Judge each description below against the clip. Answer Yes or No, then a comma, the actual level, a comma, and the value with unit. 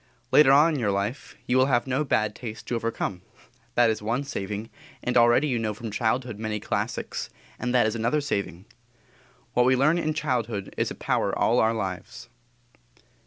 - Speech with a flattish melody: No, average, 3.3 semitones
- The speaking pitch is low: Yes, low, 120 Hz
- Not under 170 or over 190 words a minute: Yes, average, 185 wpm